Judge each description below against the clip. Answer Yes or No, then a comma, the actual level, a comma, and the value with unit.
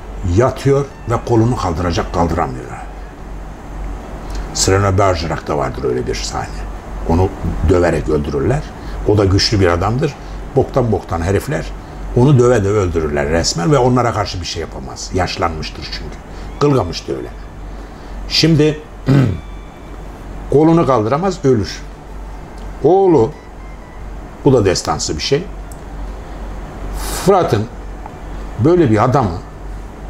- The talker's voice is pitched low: Yes, very low, 90 Hz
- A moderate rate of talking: Yes, average, 105 wpm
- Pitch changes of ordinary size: No, wide, 7.7 semitones